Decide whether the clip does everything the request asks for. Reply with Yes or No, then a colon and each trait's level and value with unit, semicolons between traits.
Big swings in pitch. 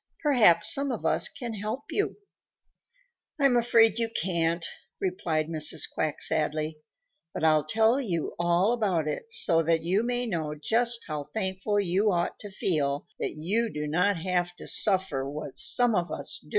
Yes: wide, 5.9 semitones